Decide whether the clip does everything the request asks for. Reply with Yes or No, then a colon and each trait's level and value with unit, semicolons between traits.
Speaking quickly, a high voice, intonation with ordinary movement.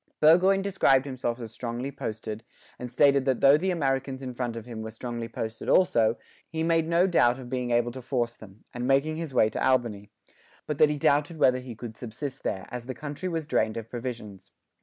No: fast, 210 wpm; low, 125 Hz; average, 4.0 semitones